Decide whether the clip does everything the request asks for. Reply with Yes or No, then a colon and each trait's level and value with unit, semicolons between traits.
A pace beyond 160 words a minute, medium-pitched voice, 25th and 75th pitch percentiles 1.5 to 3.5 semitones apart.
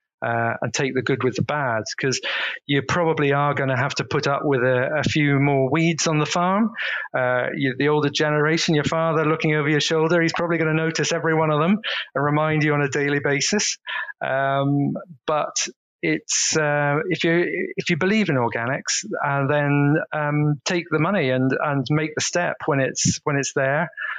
Yes: average, 200 wpm; medium, 150 Hz; narrow, 2.5 semitones